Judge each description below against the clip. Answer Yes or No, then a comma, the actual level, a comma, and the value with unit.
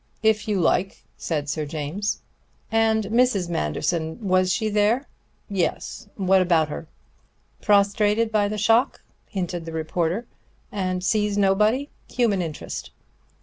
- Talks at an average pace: No, slow, 125 wpm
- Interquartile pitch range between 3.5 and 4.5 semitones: Yes, average, 3.8 semitones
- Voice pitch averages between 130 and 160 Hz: No, high, 200 Hz